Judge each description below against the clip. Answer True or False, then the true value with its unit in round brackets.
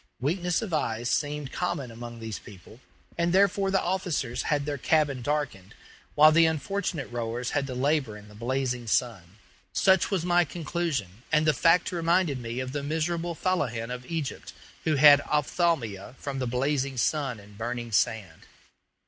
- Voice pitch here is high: False (140 Hz)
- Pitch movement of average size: False (5.7 semitones)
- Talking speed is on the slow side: False (165 wpm)